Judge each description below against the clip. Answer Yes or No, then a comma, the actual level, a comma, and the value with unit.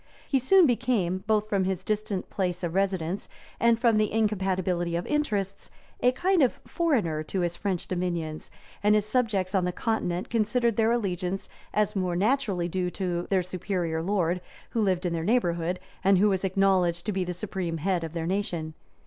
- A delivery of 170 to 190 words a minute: Yes, average, 185 wpm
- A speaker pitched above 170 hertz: Yes, high, 190 Hz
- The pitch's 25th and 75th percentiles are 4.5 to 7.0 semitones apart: No, average, 3.4 semitones